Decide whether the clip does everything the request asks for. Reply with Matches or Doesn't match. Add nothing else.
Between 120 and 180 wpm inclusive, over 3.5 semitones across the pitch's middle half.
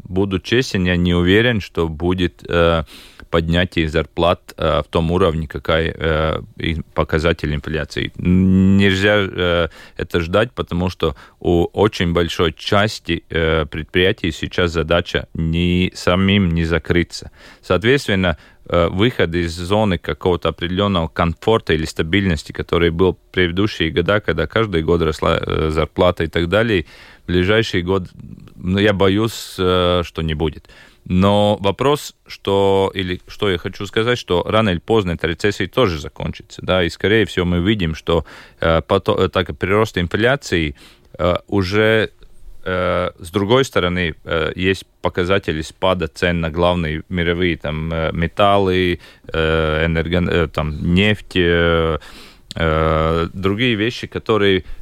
Doesn't match